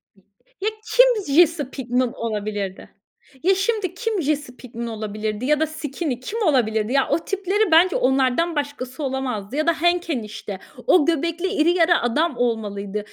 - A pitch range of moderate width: No, wide, 6.6 semitones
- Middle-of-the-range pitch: No, very high, 285 Hz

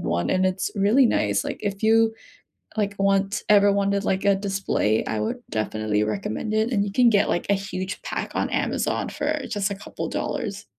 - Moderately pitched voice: No, high, 200 Hz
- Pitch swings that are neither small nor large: No, narrow, 2.2 semitones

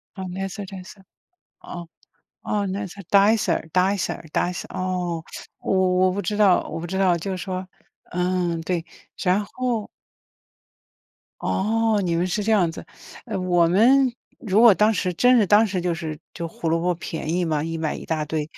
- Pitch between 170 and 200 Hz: Yes, medium, 185 Hz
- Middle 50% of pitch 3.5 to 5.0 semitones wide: No, average, 3.1 semitones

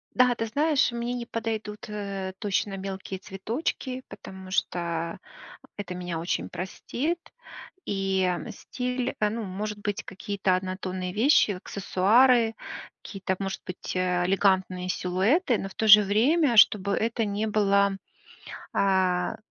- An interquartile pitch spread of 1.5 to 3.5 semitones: Yes, average, 3.2 semitones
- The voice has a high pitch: Yes, high, 200 Hz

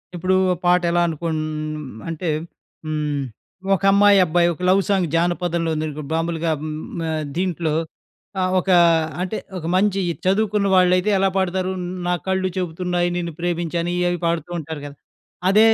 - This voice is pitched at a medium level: Yes, medium, 175 Hz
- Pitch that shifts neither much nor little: No, narrow, 2.3 semitones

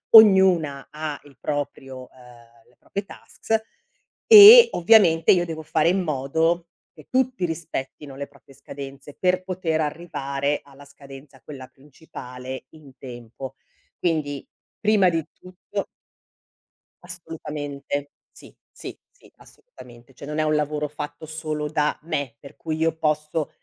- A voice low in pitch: No, medium, 150 Hz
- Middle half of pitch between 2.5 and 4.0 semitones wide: Yes, average, 3.5 semitones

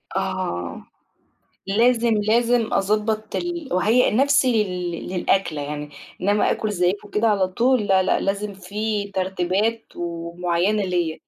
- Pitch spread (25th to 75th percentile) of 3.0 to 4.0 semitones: Yes, average, 3.7 semitones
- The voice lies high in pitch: Yes, high, 200 Hz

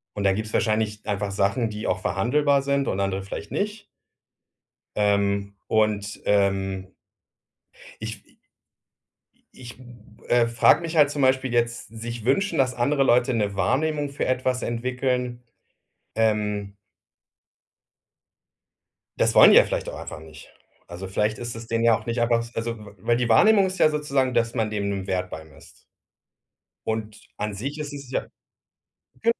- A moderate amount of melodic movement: Yes, average, 4.1 semitones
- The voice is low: Yes, low, 115 Hz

